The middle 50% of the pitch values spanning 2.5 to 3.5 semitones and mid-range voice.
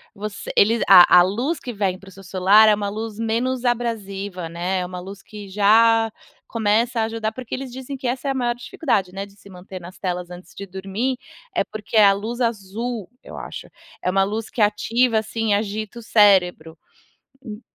No: average, 3.1 semitones; high, 210 Hz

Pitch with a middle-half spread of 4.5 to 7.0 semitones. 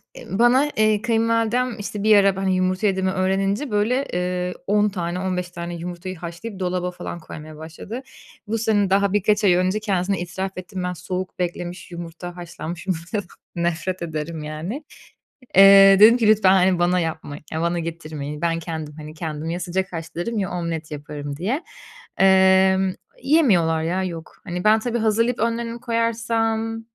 No: average, 3.8 semitones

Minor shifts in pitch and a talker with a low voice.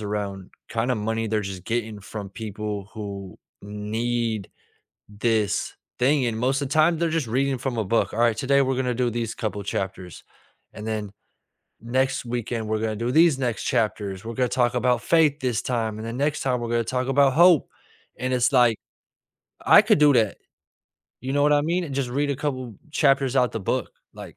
No: average, 3.7 semitones; low, 120 Hz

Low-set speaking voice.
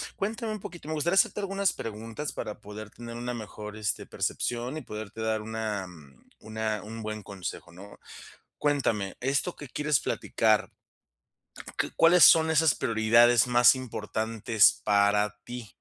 Yes: low, 115 Hz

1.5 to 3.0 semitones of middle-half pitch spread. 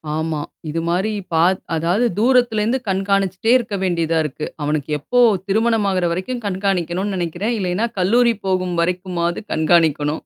No: average, 4.0 semitones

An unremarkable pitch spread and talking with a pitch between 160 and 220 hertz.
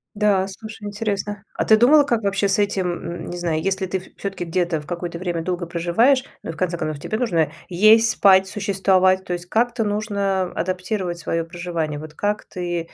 Yes: average, 3.1 semitones; high, 190 Hz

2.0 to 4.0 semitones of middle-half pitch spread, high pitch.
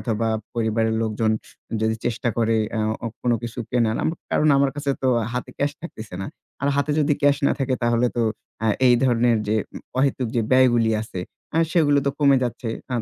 No: average, 3.5 semitones; low, 120 Hz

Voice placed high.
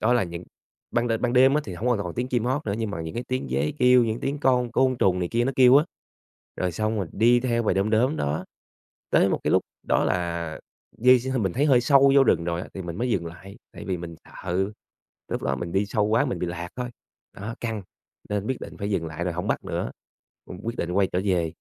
No: low, 110 Hz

